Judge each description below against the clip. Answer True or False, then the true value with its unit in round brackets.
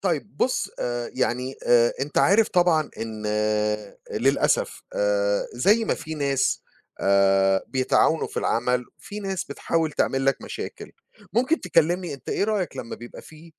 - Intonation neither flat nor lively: False (8.1 semitones)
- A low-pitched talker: False (155 Hz)